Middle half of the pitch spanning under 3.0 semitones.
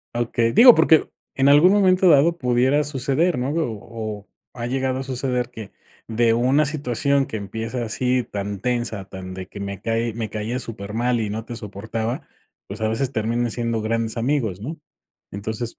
No: average, 3.3 semitones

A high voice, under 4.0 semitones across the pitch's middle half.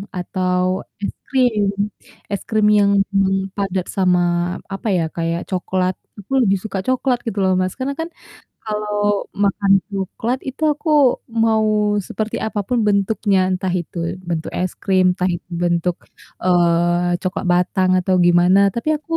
Yes: high, 195 Hz; average, 2.8 semitones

